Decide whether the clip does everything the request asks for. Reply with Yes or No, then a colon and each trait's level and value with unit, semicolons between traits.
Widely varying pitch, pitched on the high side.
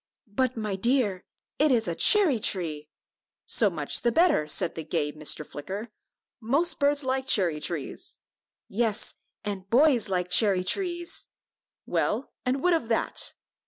Yes: wide, 6.9 semitones; high, 220 Hz